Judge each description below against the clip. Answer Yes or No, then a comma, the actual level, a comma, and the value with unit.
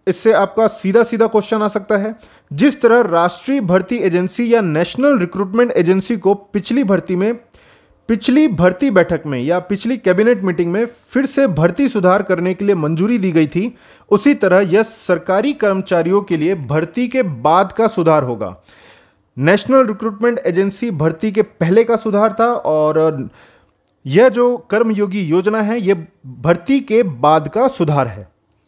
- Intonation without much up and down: No, average, 5.0 semitones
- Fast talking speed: No, average, 160 wpm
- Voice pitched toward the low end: No, high, 200 Hz